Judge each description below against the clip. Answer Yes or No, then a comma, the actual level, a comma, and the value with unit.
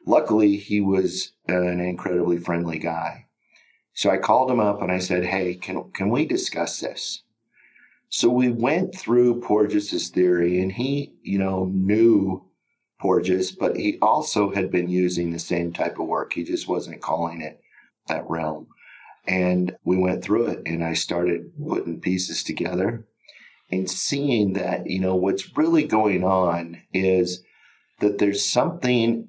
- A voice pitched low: Yes, very low, 95 Hz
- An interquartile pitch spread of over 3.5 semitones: No, average, 2.8 semitones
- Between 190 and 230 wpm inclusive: No, average, 155 wpm